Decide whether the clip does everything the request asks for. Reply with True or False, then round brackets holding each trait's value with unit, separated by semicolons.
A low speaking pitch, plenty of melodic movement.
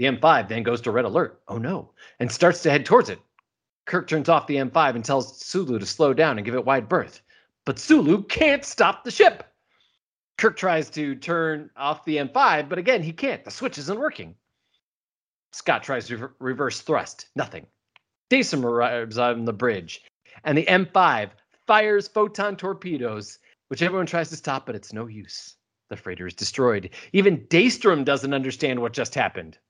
False (150 Hz; 6.7 semitones)